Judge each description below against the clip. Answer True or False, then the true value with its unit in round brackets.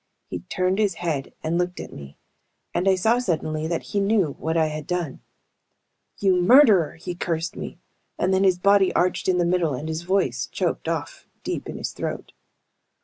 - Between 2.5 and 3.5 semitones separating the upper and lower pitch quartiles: True (3.1 semitones)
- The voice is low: False (180 Hz)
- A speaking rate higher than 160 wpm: True (190 wpm)